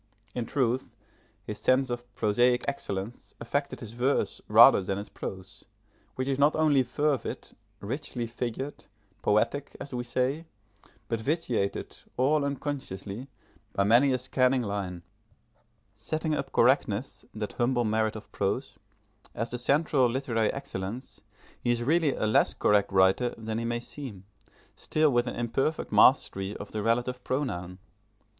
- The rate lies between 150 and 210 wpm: No, average, 140 wpm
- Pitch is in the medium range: No, low, 120 Hz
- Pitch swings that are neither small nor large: Yes, average, 4.0 semitones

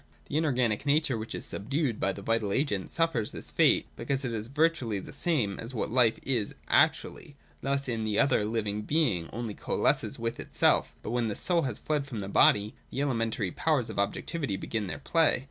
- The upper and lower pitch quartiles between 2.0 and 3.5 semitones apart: No, average, 5.0 semitones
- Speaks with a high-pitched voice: No, low, 115 Hz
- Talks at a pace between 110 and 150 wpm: No, average, 200 wpm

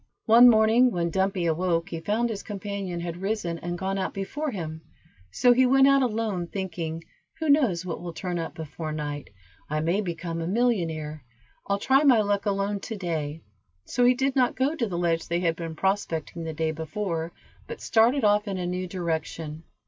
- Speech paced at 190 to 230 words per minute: Yes, average, 195 wpm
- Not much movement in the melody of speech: No, average, 4.8 semitones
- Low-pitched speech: No, medium, 185 Hz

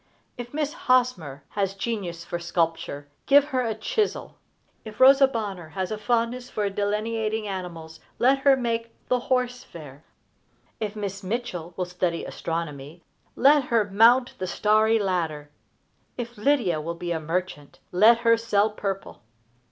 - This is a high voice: Yes, high, 210 Hz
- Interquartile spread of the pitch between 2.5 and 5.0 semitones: No, wide, 5.6 semitones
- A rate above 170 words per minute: No, average, 145 wpm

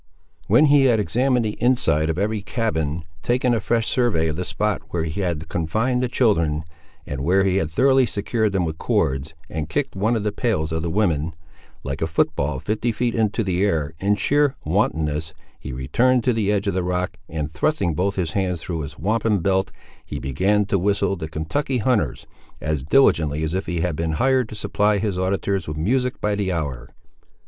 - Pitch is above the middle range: No, very low, 95 Hz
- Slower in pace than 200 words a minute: No, fast, 205 wpm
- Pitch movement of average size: No, wide, 5.7 semitones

